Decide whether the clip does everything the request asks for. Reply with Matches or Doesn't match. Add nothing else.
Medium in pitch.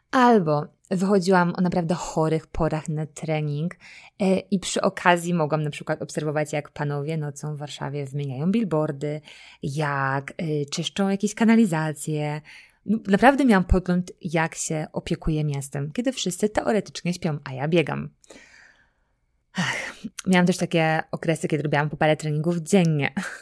Matches